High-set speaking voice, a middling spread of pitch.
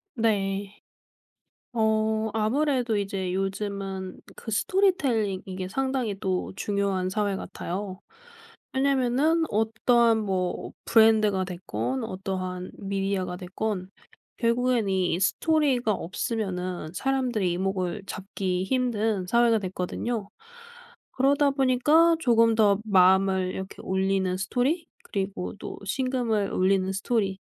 Yes: high, 205 Hz; average, 4.0 semitones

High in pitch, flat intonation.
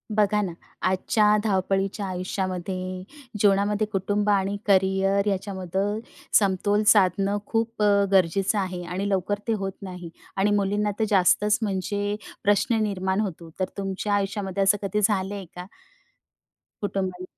Yes: high, 195 Hz; narrow, 1.5 semitones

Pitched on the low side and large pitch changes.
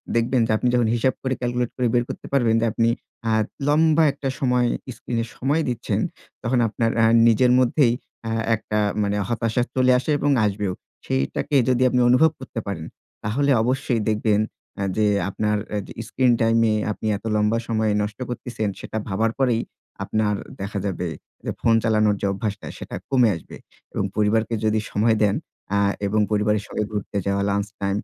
No: low, 115 Hz; average, 2.9 semitones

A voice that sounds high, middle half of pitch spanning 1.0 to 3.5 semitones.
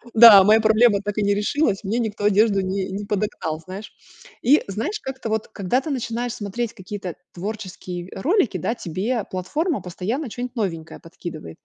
No: high, 210 Hz; average, 3.9 semitones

